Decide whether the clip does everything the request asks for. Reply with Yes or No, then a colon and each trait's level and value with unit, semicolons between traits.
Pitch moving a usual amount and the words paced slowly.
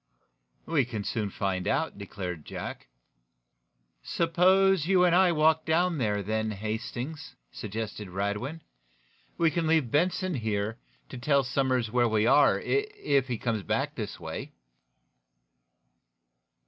No: wide, 7.3 semitones; slow, 125 wpm